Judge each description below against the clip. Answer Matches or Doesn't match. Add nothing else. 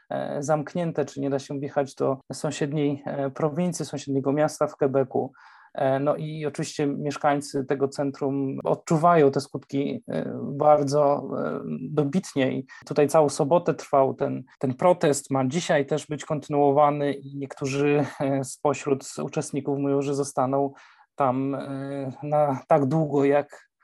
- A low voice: Doesn't match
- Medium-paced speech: Matches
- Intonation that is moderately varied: Doesn't match